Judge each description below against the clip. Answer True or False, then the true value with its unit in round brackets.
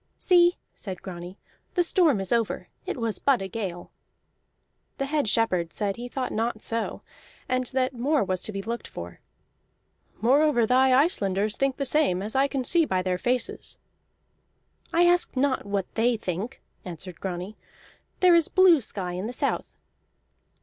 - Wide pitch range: True (6.1 semitones)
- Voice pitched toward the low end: False (235 Hz)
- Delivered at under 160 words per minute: False (165 wpm)